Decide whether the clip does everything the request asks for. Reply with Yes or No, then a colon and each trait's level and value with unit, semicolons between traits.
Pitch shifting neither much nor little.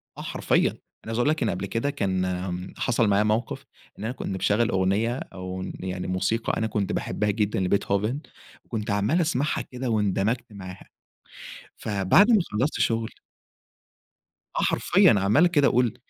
Yes: average, 4.0 semitones